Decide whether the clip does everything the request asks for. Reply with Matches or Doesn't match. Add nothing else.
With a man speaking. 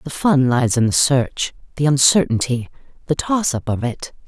Doesn't match